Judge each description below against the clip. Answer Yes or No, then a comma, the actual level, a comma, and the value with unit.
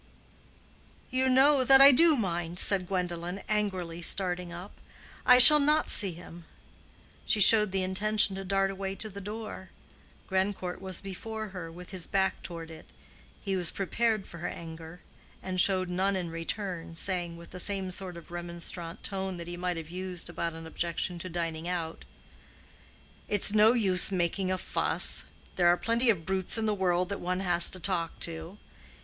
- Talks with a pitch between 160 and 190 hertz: Yes, medium, 185 Hz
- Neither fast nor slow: Yes, average, 175 wpm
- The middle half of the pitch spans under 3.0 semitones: Yes, narrow, 2.6 semitones